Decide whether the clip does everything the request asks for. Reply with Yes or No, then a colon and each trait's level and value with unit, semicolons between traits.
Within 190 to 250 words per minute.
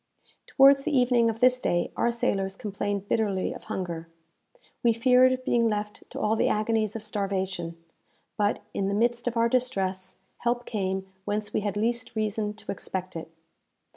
No: average, 170 wpm